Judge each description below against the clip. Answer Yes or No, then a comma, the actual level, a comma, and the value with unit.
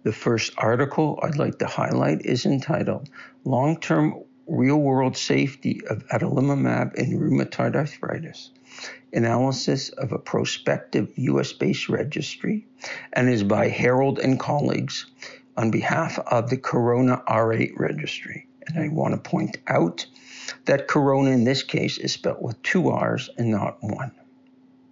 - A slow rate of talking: Yes, slow, 130 wpm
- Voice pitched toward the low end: Yes, low, 130 Hz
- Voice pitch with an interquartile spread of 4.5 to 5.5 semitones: Yes, average, 4.8 semitones